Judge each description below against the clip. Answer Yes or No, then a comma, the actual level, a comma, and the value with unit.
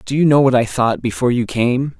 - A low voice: Yes, low, 125 Hz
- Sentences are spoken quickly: Yes, fast, 270 wpm